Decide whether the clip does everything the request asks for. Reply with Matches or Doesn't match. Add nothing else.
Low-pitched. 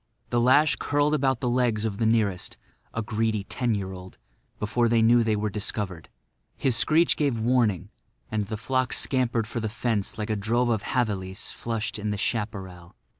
Matches